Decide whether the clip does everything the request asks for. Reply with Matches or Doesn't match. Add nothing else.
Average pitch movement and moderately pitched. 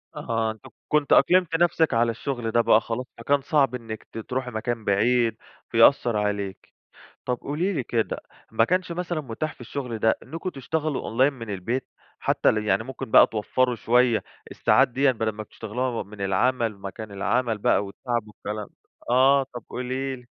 Doesn't match